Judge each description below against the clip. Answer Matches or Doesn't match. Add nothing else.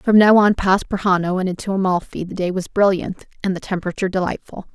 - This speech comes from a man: Doesn't match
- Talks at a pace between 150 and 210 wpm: Matches